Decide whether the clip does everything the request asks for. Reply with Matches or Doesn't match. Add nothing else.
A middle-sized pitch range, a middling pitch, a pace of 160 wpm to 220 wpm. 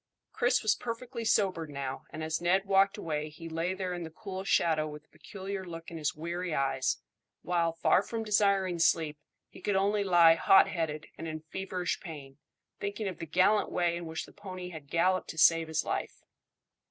Matches